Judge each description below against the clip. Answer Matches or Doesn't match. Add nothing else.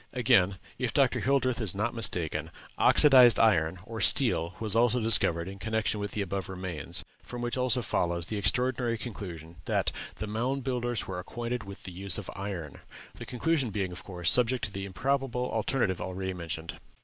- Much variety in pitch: Doesn't match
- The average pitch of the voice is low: Matches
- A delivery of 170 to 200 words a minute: Matches